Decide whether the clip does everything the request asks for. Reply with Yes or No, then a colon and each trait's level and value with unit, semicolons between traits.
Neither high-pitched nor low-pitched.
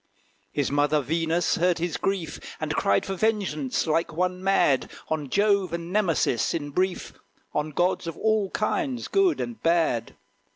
Yes: medium, 170 Hz